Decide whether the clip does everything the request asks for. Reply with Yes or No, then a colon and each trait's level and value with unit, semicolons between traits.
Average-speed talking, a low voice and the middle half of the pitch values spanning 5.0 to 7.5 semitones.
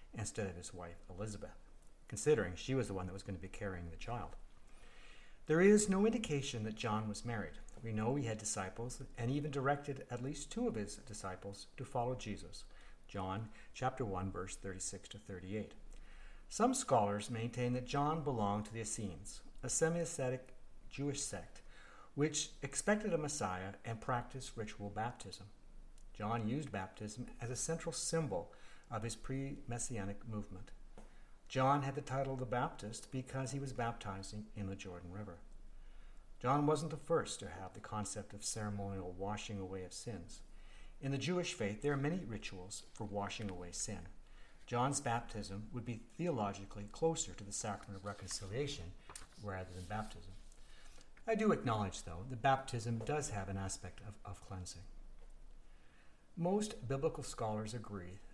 Yes: average, 160 wpm; low, 110 Hz; average, 5.3 semitones